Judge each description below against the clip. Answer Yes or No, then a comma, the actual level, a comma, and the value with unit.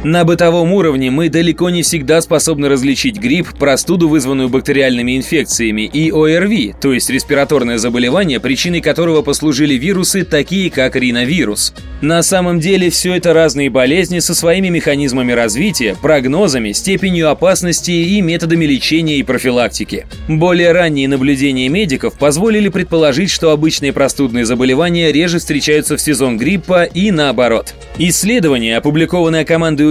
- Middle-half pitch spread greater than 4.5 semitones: No, average, 4.0 semitones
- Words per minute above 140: No, average, 130 wpm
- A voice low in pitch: No, medium, 155 Hz